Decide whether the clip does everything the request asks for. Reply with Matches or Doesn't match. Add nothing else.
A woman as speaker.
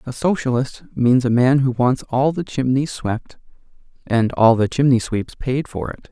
Doesn't match